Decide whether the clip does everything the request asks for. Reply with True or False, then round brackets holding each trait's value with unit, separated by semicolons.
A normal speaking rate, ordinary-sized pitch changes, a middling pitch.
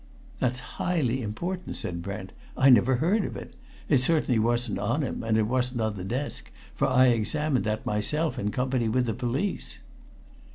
False (175 wpm; 3.6 semitones; 125 Hz)